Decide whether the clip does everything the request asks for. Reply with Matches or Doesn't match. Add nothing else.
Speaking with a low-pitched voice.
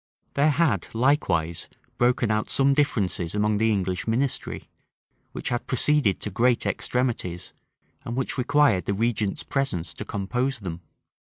Matches